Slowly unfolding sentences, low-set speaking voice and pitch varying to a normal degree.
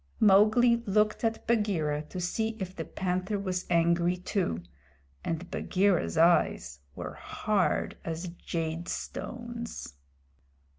No: slow, 115 wpm; medium, 185 Hz; average, 3.9 semitones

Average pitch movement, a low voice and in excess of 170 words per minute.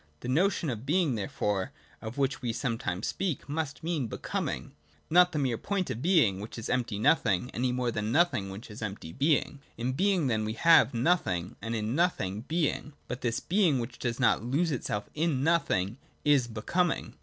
No: wide, 6.5 semitones; low, 125 Hz; average, 190 wpm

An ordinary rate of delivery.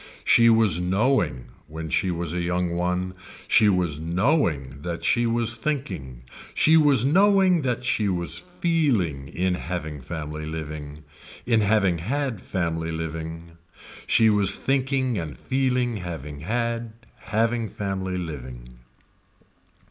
No: slow, 125 wpm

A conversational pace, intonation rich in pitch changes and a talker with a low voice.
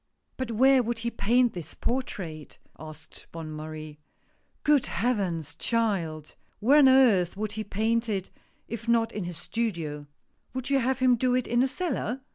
No: average, 180 wpm; wide, 6.7 semitones; high, 225 Hz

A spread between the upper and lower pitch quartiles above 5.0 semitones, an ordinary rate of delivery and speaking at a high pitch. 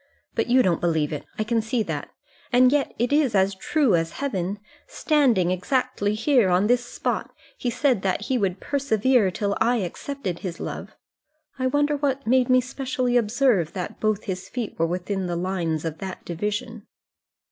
Yes: wide, 5.6 semitones; average, 180 wpm; high, 215 Hz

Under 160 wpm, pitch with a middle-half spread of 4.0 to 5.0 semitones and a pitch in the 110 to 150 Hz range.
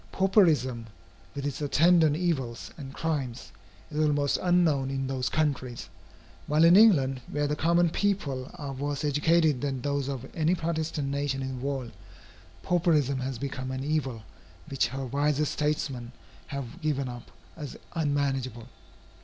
No: average, 145 wpm; average, 2.9 semitones; medium, 140 Hz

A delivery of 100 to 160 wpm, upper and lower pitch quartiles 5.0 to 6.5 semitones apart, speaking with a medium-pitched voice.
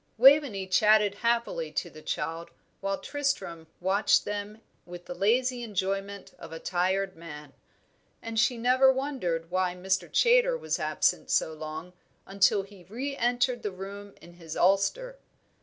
No: average, 145 wpm; wide, 5.4 semitones; high, 195 Hz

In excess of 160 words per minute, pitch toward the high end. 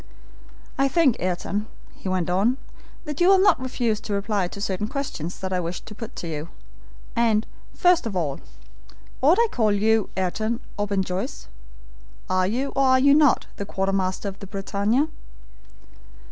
Yes: average, 175 wpm; high, 210 Hz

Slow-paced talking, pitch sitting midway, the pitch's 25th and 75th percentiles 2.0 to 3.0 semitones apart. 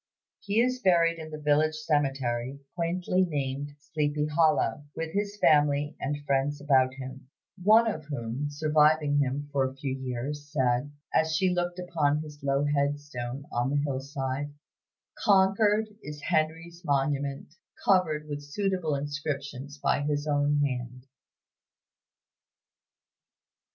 Yes: slow, 130 wpm; medium, 145 Hz; narrow, 2.4 semitones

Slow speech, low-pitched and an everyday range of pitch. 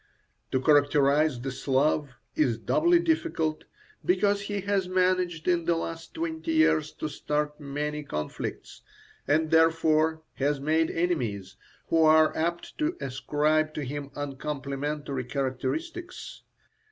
No: slow, 120 wpm; medium, 155 Hz; average, 3.7 semitones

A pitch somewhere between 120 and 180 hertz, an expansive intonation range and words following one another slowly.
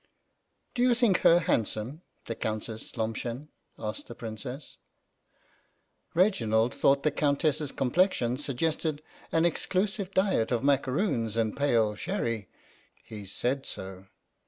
Yes: low, 135 Hz; wide, 6.6 semitones; slow, 130 wpm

